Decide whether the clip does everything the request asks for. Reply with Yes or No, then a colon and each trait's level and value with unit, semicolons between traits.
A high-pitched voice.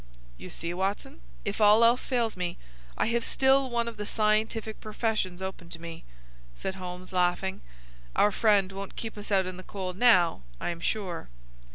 Yes: high, 195 Hz